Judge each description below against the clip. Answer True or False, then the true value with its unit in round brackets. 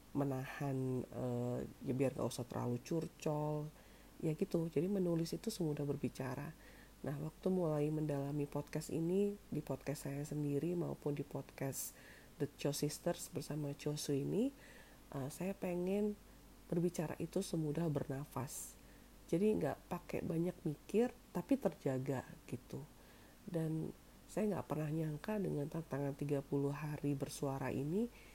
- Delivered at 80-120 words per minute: False (130 wpm)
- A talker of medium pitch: True (150 Hz)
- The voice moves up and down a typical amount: True (3.6 semitones)